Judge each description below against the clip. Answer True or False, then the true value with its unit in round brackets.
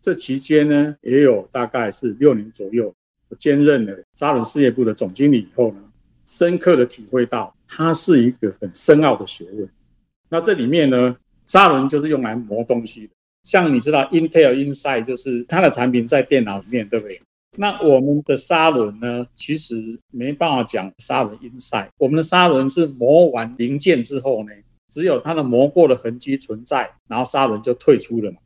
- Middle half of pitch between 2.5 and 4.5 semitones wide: True (4.0 semitones)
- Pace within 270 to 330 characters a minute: True (300 characters per minute)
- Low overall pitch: True (125 Hz)